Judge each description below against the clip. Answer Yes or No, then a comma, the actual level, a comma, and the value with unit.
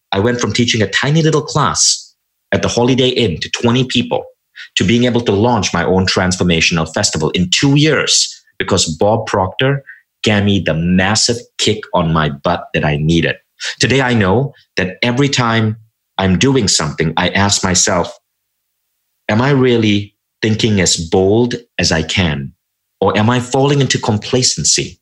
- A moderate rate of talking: Yes, average, 165 wpm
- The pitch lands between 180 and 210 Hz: No, low, 110 Hz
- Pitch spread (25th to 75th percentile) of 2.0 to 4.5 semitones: No, wide, 5.5 semitones